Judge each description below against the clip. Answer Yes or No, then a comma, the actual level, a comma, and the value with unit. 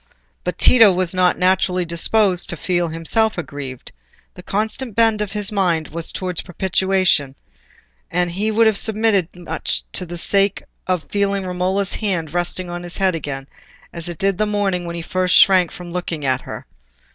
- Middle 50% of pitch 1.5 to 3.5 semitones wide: Yes, narrow, 2.6 semitones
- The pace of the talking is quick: No, average, 180 wpm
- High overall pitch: No, medium, 180 Hz